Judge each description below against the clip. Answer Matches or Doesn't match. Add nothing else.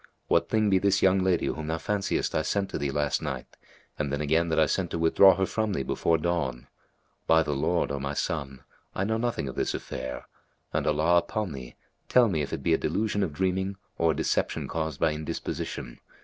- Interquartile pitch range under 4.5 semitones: Doesn't match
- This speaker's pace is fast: Matches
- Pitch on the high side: Doesn't match